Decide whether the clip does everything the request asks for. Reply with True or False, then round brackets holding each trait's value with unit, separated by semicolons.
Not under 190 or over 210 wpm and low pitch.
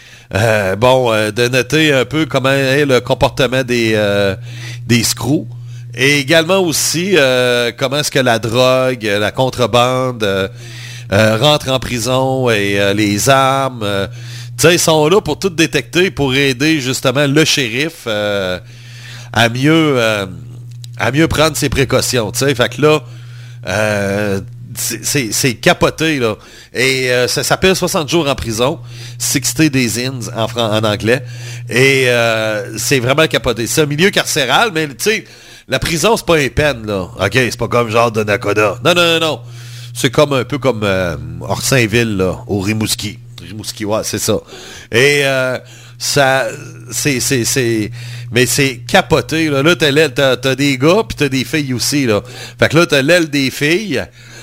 False (175 wpm; 125 Hz)